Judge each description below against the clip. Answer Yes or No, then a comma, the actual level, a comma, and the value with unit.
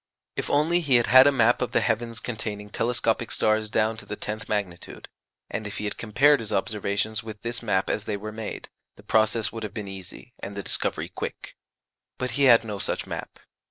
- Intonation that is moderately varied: No, narrow, 2.3 semitones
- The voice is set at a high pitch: No, low, 110 Hz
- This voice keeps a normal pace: No, fast, 210 wpm